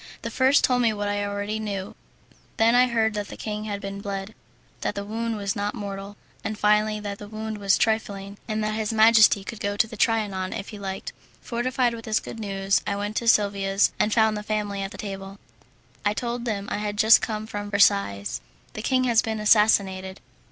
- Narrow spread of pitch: Yes, narrow, 1.6 semitones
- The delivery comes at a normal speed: No, fast, 210 wpm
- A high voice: Yes, high, 210 Hz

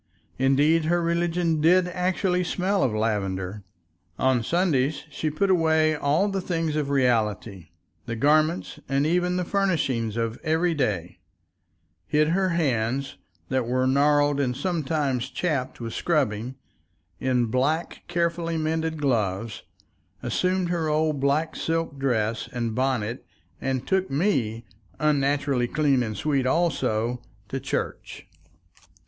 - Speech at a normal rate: No, slow, 125 wpm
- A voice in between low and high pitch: Yes, medium, 145 Hz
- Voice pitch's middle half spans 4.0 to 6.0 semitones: Yes, average, 5.0 semitones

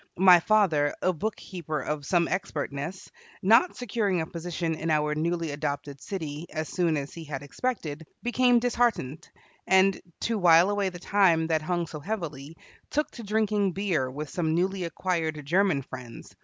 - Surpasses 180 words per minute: No, average, 160 wpm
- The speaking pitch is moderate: Yes, medium, 170 Hz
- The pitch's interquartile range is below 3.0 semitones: No, average, 4.4 semitones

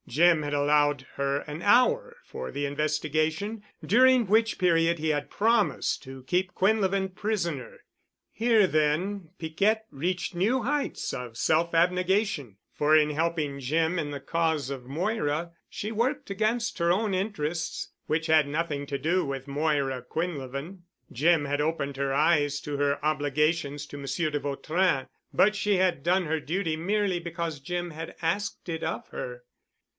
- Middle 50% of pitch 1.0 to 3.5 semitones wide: No, average, 4.6 semitones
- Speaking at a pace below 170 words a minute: Yes, average, 155 wpm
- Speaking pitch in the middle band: Yes, medium, 165 Hz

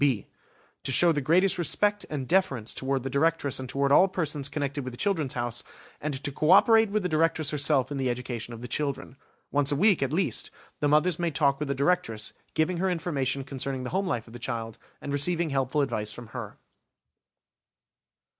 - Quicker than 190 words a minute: Yes, average, 200 wpm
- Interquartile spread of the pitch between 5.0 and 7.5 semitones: No, average, 4.1 semitones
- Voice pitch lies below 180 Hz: Yes, medium, 140 Hz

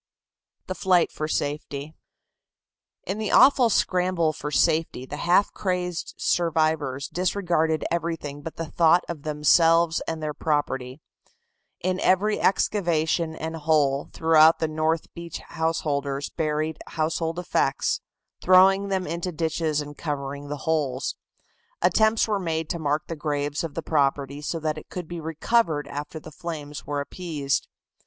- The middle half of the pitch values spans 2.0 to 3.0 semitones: Yes, narrow, 2.6 semitones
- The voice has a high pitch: No, medium, 160 Hz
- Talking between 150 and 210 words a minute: No, average, 140 wpm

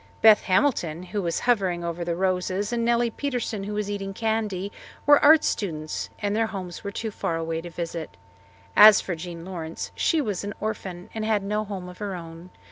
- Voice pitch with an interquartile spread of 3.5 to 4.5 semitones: Yes, average, 3.8 semitones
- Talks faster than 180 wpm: Yes, average, 200 wpm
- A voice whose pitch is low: No, high, 195 Hz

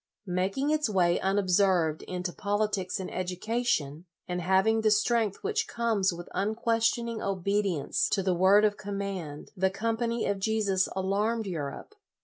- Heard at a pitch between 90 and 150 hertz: No, high, 200 Hz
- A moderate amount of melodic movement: Yes, average, 3.3 semitones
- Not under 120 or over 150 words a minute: Yes, average, 145 wpm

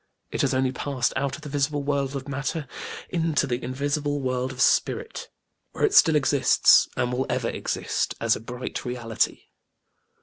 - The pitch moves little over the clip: Yes, narrow, 2.3 semitones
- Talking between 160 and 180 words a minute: Yes, average, 170 wpm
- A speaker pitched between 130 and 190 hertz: Yes, low, 135 Hz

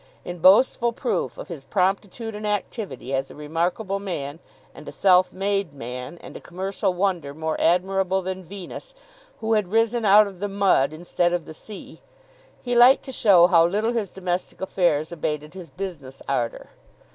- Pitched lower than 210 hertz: Yes, medium, 185 Hz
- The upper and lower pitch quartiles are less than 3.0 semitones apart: No, average, 3.8 semitones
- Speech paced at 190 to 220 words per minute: No, average, 170 wpm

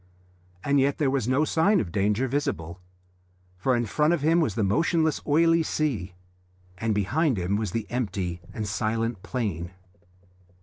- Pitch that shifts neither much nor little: No, wide, 6.9 semitones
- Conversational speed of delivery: Yes, average, 160 wpm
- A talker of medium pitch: No, low, 120 Hz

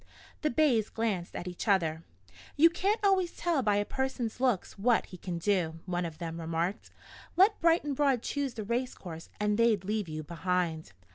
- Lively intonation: Yes, wide, 7.3 semitones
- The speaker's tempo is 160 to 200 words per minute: Yes, average, 190 wpm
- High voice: Yes, high, 210 Hz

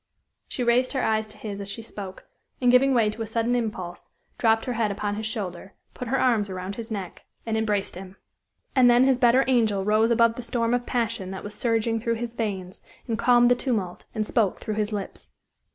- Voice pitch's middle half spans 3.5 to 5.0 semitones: No, average, 2.7 semitones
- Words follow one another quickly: Yes, fast, 215 wpm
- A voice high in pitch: Yes, high, 225 Hz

